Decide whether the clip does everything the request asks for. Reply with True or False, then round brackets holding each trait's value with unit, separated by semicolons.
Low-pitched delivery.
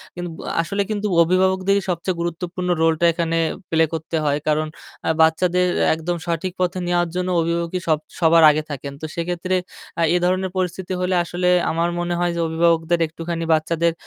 False (170 Hz)